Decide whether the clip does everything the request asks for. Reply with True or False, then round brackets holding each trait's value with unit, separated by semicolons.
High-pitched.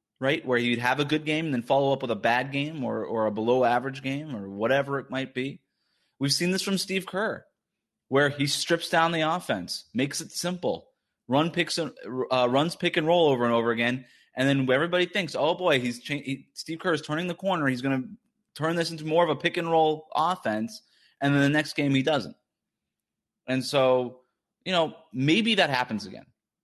False (140 Hz)